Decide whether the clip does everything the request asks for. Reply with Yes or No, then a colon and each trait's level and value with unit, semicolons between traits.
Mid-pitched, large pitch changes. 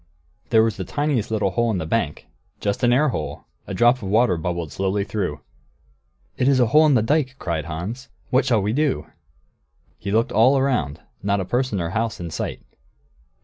No: low, 110 Hz; wide, 6.2 semitones